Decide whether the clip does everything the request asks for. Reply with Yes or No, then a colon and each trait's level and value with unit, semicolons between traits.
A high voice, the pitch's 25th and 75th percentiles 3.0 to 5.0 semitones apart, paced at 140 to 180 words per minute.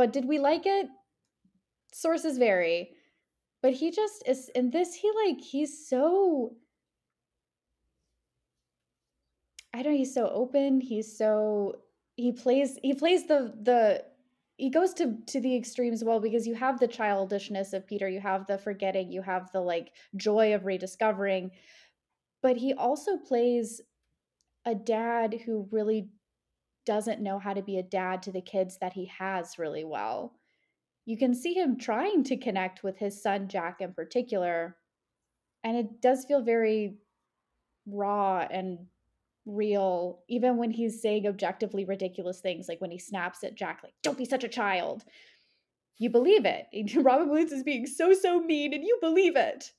No: high, 225 Hz; wide, 5.5 semitones; average, 160 wpm